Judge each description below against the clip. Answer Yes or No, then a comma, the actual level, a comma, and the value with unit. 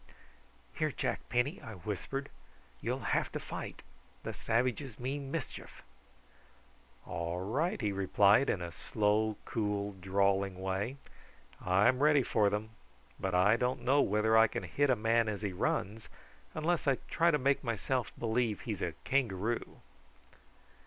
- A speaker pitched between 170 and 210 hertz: No, low, 110 Hz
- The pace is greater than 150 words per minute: No, average, 145 wpm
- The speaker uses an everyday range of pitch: Yes, average, 4.5 semitones